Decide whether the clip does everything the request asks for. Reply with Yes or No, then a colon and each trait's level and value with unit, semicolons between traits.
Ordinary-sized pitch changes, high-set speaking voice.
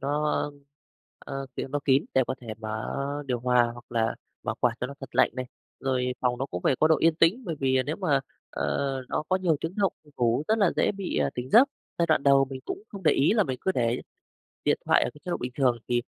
No: average, 4.6 semitones; low, 135 Hz